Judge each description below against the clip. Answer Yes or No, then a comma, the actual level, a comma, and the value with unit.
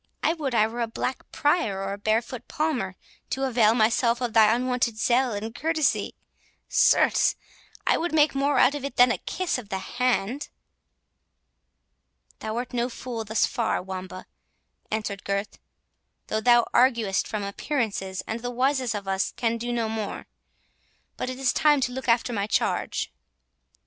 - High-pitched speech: Yes, high, 235 Hz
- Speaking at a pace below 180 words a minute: Yes, average, 160 wpm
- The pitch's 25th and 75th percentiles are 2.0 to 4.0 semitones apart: Yes, average, 3.1 semitones